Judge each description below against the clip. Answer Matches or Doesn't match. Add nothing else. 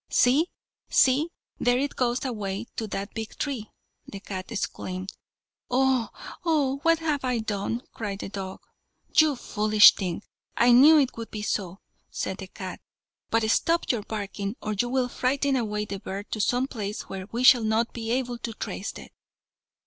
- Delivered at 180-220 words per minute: Doesn't match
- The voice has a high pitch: Matches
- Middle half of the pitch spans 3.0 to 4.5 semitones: Matches